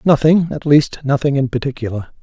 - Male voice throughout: Yes, male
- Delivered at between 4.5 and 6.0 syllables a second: Yes, 5.6 syllables/s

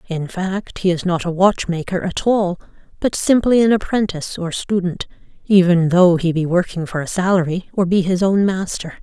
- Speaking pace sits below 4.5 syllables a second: No, 5.0 syllables/s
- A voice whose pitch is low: No, medium, 180 Hz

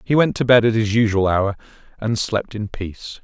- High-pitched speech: No, low, 110 Hz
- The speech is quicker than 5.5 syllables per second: No, 5.2 syllables/s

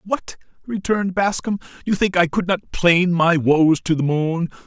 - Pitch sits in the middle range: Yes, medium, 180 Hz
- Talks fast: No, average, 180 wpm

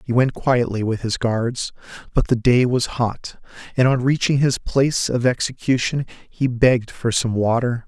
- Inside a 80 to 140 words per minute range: No, average, 175 wpm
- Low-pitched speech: Yes, low, 120 Hz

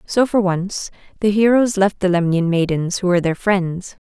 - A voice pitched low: No, high, 190 Hz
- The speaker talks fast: No, average, 190 wpm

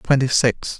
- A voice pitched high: No, low, 125 Hz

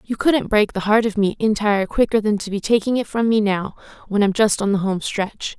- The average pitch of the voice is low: No, high, 210 Hz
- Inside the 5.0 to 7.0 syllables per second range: Yes, 5.5 syllables/s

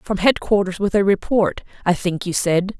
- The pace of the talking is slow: No, average, 195 wpm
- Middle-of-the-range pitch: No, high, 195 Hz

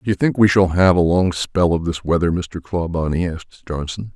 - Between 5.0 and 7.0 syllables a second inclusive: Yes, 5.2 syllables/s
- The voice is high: No, very low, 90 Hz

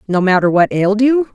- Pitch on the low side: No, high, 205 Hz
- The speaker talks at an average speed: No, fast, 225 wpm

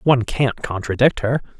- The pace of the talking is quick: No, average, 150 wpm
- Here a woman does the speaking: No, male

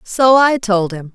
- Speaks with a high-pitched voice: Yes, high, 220 Hz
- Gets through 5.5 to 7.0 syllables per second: No, 3.8 syllables/s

